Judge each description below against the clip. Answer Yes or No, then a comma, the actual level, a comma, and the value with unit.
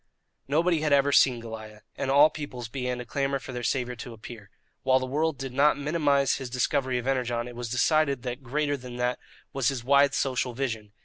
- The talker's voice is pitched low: Yes, low, 130 Hz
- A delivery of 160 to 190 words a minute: No, fast, 205 wpm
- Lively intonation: No, narrow, 2.5 semitones